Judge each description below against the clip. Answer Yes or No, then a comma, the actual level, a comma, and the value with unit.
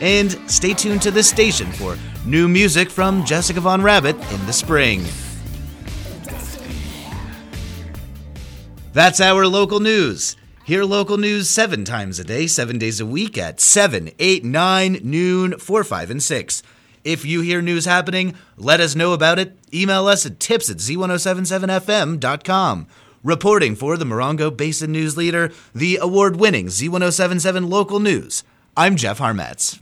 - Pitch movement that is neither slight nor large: No, wide, 7.9 semitones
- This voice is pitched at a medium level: Yes, medium, 170 Hz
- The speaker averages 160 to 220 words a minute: No, average, 145 wpm